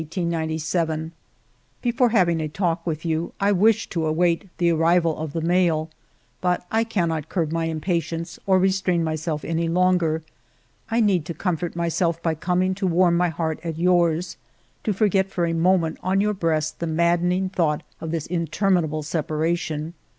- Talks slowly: No, average, 165 wpm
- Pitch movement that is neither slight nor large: No, narrow, 2.1 semitones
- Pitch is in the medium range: Yes, medium, 170 Hz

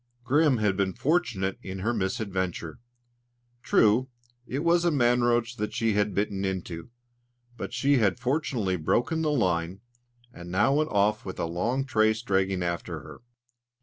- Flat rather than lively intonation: No, average, 5.0 semitones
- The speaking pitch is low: Yes, low, 110 Hz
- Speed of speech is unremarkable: Yes, average, 155 wpm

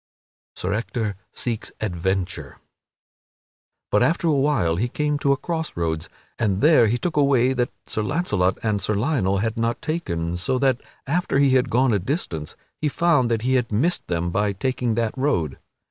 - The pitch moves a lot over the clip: Yes, wide, 6.2 semitones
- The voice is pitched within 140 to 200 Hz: No, low, 115 Hz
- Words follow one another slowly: No, average, 185 wpm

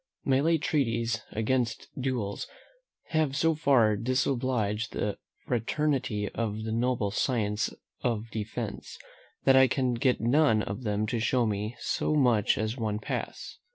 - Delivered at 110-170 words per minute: Yes, average, 140 wpm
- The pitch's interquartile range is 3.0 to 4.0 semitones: Yes, average, 3.5 semitones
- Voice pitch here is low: Yes, low, 115 Hz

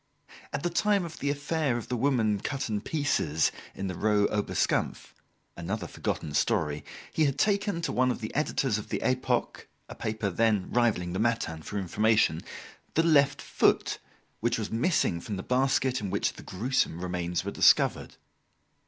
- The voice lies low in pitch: Yes, low, 115 Hz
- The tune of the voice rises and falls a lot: Yes, wide, 6.2 semitones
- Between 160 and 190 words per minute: Yes, average, 170 wpm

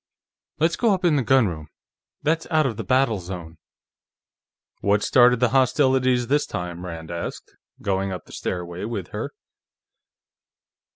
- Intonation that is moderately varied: No, wide, 7.0 semitones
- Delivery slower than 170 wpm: Yes, average, 140 wpm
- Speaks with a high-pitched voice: No, low, 115 Hz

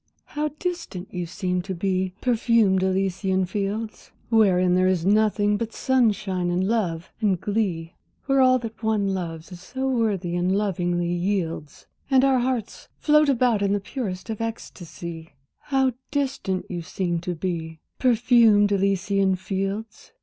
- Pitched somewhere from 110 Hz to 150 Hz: No, high, 195 Hz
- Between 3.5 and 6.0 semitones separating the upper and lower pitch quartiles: Yes, average, 3.9 semitones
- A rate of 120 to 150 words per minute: Yes, average, 145 wpm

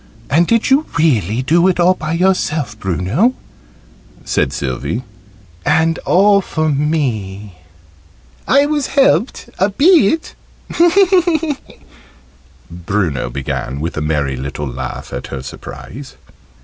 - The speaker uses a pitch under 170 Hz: Yes, medium, 140 Hz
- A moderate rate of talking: No, slow, 110 wpm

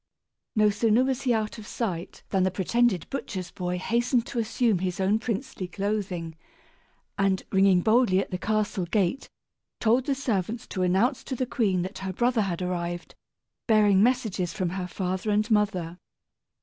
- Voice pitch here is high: Yes, high, 200 Hz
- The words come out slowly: No, average, 165 wpm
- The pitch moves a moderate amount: Yes, average, 4.0 semitones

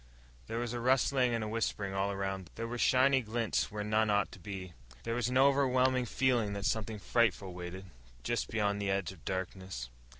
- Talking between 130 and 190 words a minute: No, average, 200 wpm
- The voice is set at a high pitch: No, low, 110 Hz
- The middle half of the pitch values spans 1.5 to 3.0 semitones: No, average, 3.9 semitones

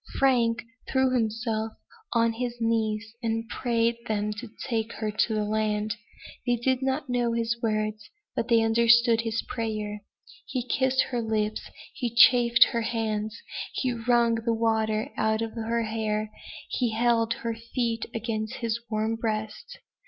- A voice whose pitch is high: Yes, high, 230 Hz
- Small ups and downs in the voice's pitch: Yes, narrow, 1.5 semitones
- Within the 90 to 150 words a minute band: Yes, average, 145 wpm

